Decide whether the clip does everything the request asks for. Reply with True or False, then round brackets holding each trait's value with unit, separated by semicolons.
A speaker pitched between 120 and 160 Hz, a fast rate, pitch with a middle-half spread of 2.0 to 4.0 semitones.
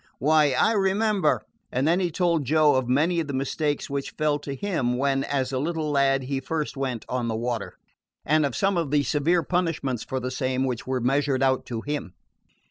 True (140 Hz; 215 wpm; 3.4 semitones)